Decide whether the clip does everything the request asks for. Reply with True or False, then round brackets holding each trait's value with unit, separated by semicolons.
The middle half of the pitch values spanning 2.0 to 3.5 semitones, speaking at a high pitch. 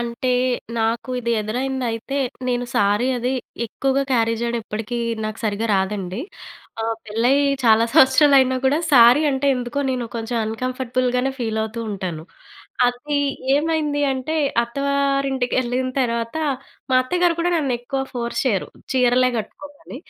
True (2.8 semitones; 250 Hz)